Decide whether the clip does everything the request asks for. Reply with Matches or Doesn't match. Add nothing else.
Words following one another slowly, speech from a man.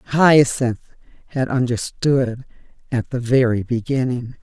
Doesn't match